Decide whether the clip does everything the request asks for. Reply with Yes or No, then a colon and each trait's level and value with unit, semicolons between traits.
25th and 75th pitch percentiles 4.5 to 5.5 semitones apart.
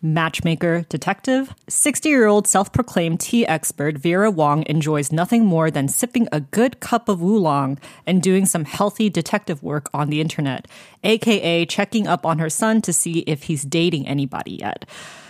Yes: average, 5.2 semitones